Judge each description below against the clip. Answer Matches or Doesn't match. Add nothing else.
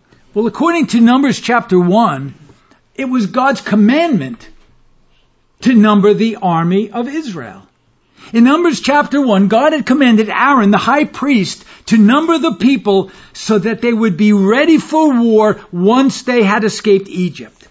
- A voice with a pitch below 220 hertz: Doesn't match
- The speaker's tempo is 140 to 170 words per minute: Matches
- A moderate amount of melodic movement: Matches